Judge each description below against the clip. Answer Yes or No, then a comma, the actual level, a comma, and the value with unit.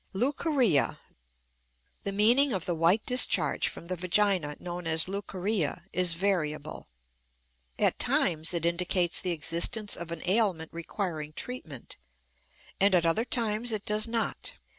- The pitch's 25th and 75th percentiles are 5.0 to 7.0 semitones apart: No, average, 4.2 semitones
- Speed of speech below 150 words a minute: Yes, slow, 135 wpm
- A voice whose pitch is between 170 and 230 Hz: Yes, medium, 185 Hz